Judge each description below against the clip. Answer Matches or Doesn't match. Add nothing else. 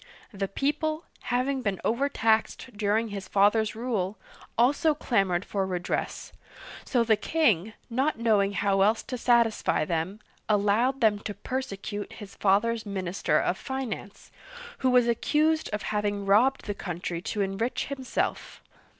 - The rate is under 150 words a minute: Matches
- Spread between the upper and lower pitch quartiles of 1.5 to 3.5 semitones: Doesn't match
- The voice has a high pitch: Matches